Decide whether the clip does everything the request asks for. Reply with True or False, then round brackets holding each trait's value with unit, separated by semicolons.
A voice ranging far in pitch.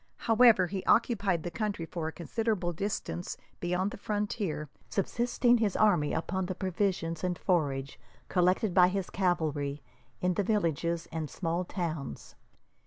False (3.7 semitones)